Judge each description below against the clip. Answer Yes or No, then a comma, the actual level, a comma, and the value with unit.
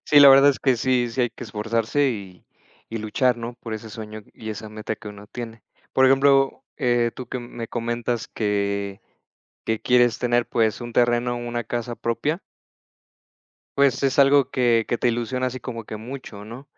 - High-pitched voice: No, low, 120 Hz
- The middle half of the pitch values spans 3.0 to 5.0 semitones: No, narrow, 2.5 semitones